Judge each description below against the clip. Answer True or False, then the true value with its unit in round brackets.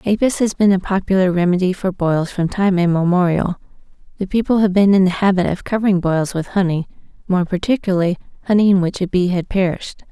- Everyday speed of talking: True (190 wpm)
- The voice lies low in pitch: False (185 Hz)